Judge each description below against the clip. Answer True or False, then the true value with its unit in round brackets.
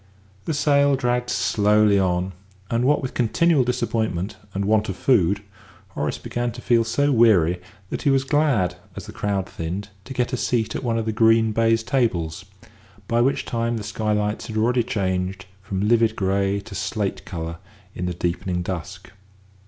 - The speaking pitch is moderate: False (110 Hz)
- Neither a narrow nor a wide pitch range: True (4.0 semitones)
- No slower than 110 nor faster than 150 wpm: False (175 wpm)